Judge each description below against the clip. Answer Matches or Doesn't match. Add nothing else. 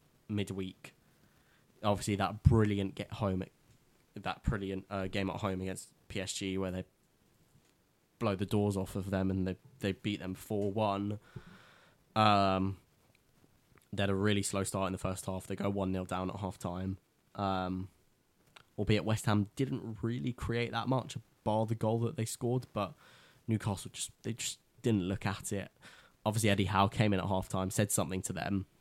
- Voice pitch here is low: Matches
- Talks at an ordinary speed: Matches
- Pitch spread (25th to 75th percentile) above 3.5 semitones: Doesn't match